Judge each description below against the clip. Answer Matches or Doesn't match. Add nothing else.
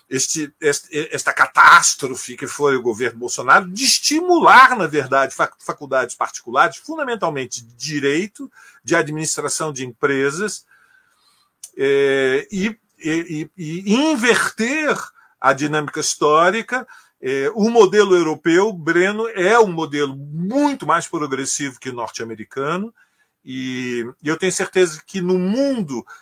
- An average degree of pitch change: Doesn't match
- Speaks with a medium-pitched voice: Matches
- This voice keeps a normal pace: Doesn't match